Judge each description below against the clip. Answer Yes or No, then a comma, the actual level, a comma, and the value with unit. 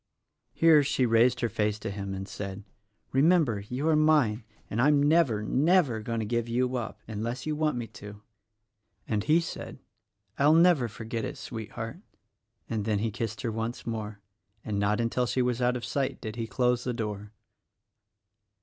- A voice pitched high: No, low, 115 Hz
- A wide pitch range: No, average, 4.0 semitones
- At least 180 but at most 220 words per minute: Yes, average, 185 wpm